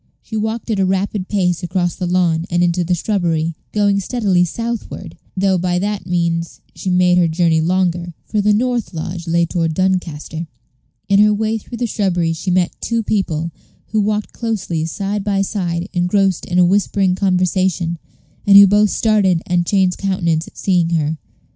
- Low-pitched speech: No, medium, 185 Hz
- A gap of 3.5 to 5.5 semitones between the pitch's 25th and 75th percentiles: No, average, 2.9 semitones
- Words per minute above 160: Yes, average, 175 wpm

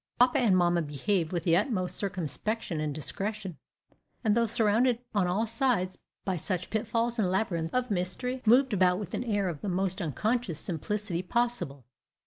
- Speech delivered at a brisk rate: No, average, 165 wpm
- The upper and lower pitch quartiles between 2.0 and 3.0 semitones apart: No, average, 4.4 semitones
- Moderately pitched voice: No, high, 195 Hz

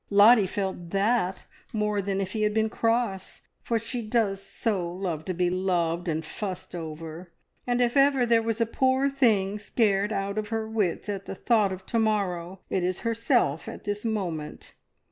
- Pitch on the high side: Yes, high, 205 Hz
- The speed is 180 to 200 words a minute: Yes, average, 185 wpm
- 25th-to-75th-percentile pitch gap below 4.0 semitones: Yes, average, 3.6 semitones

